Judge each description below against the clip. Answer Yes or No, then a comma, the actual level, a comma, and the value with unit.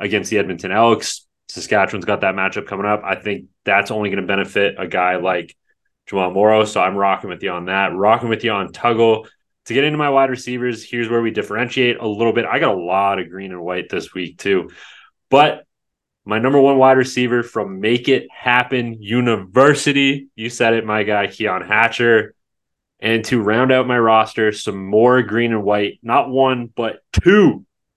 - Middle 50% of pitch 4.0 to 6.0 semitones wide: No, average, 3.4 semitones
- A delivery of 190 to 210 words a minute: Yes, average, 195 wpm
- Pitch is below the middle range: Yes, low, 110 Hz